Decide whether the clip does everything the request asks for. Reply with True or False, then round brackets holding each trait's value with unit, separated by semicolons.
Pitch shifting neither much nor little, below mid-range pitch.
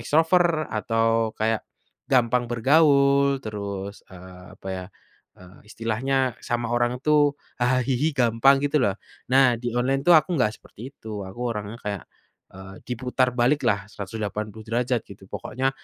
True (4.1 semitones; 120 Hz)